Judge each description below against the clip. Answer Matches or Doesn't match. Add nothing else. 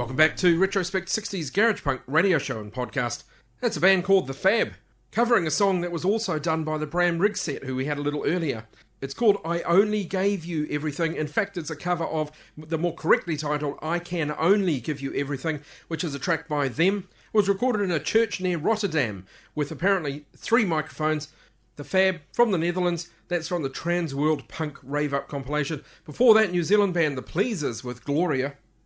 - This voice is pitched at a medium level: Matches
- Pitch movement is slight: Doesn't match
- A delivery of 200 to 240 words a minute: Matches